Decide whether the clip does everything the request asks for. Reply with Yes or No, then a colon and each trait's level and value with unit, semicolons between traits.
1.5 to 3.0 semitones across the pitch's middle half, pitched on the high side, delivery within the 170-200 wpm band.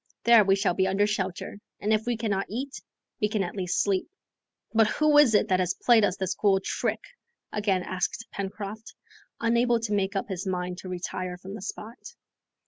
Yes: average, 2.7 semitones; high, 200 Hz; average, 195 wpm